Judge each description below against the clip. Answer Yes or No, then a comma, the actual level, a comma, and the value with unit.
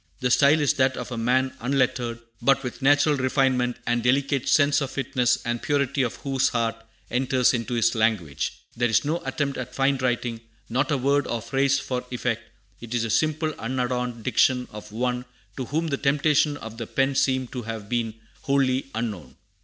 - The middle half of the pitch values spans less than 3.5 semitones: Yes, average, 2.7 semitones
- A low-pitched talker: Yes, low, 125 Hz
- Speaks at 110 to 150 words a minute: No, average, 185 wpm